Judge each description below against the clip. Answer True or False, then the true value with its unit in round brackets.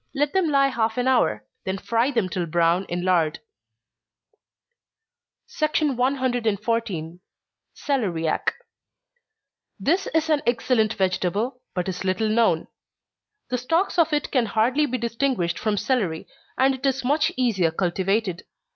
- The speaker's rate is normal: False (130 wpm)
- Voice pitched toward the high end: True (230 Hz)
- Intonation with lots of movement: True (6.3 semitones)